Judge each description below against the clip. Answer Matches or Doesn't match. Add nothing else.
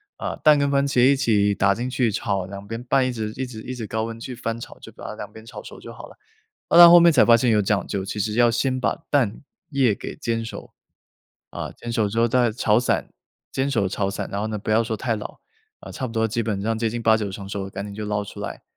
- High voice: Doesn't match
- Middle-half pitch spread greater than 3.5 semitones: Doesn't match